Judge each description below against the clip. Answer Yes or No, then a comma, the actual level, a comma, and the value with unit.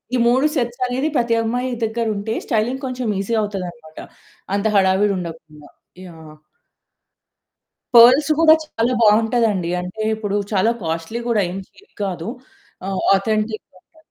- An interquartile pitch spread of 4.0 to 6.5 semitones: Yes, average, 4.3 semitones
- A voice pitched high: Yes, high, 220 Hz